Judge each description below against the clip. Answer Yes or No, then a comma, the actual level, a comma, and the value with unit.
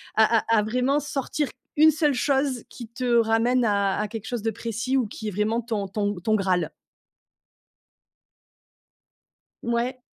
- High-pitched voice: Yes, high, 230 Hz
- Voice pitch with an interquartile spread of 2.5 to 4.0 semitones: Yes, average, 3.2 semitones